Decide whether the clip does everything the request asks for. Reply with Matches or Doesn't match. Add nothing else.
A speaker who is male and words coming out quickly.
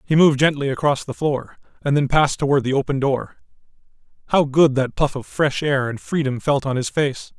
Matches